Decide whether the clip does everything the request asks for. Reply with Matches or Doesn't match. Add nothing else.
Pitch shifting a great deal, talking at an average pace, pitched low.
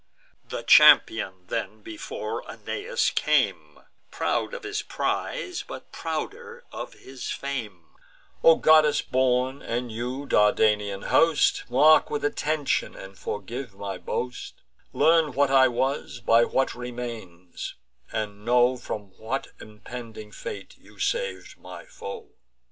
Doesn't match